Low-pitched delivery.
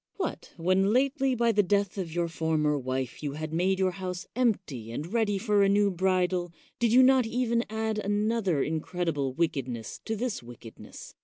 No: high, 190 Hz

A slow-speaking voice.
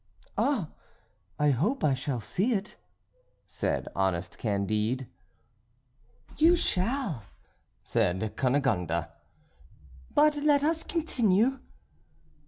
Yes: slow, 85 wpm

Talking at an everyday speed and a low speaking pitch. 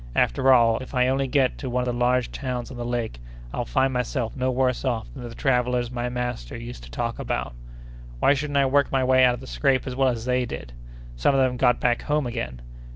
No: fast, 240 wpm; low, 125 Hz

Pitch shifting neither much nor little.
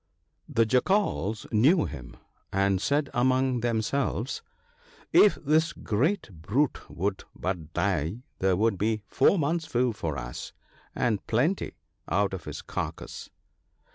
No: wide, 6.3 semitones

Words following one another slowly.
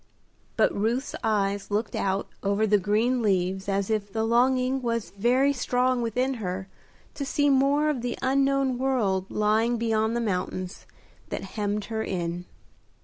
No: average, 150 wpm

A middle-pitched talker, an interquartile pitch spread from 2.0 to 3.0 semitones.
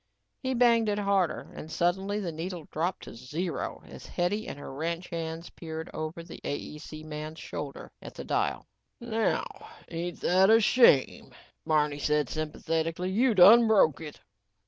No: medium, 170 Hz; average, 4.3 semitones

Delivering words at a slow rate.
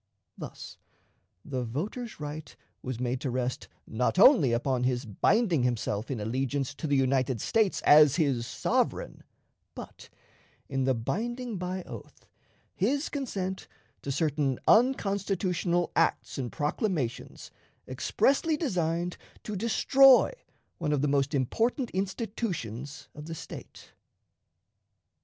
Yes: slow, 120 wpm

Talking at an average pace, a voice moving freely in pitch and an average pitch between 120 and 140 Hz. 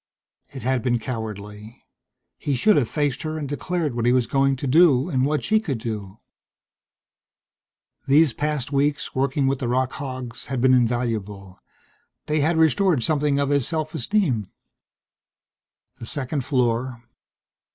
No: average, 150 wpm; average, 3.7 semitones; low, 135 Hz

